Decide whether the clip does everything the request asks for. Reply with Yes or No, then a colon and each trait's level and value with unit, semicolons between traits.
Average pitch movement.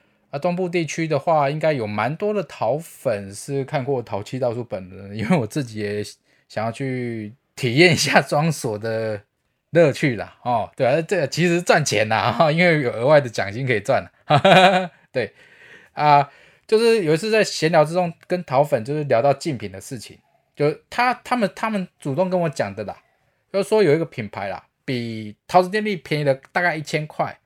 No: wide, 6.7 semitones